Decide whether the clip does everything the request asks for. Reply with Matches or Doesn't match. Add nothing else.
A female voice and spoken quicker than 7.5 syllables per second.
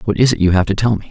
Doesn't match